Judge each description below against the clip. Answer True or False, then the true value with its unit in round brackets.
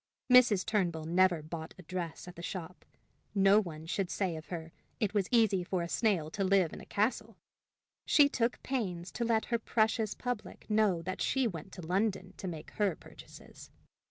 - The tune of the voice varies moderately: True (4.2 semitones)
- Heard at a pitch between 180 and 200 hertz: True (190 Hz)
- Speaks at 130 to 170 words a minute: False (185 wpm)